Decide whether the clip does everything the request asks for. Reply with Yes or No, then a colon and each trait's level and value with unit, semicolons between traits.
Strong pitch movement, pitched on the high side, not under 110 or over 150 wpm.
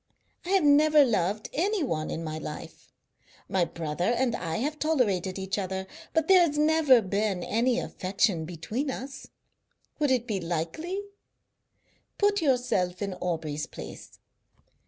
Yes: wide, 8.8 semitones; high, 215 Hz; average, 140 wpm